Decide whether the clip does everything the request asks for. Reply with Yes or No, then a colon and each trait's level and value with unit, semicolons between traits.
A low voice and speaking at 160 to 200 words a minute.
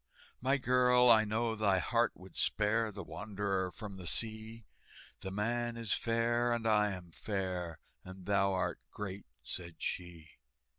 No: low, 105 Hz; average, 150 wpm